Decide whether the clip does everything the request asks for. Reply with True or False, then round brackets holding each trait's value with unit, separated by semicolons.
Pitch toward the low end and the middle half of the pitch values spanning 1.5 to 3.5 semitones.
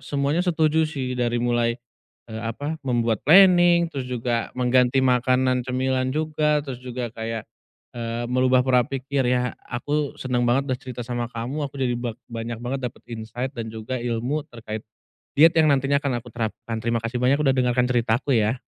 True (125 Hz; 2.6 semitones)